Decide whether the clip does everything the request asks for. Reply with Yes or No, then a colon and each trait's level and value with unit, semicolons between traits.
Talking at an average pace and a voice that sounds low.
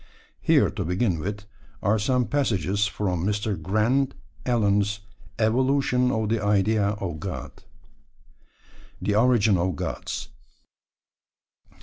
No: slow, 105 wpm; low, 105 Hz